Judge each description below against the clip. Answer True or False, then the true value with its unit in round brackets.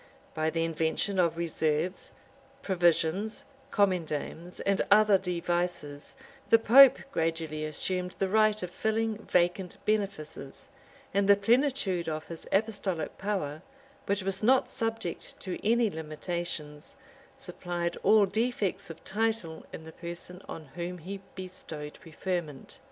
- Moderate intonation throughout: True (3.9 semitones)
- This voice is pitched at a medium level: True (180 Hz)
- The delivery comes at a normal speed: False (125 wpm)